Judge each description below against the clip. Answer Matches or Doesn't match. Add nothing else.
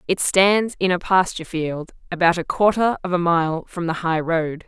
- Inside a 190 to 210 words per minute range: Matches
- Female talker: Matches